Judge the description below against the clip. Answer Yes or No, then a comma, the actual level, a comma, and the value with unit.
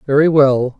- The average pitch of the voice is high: No, medium, 140 Hz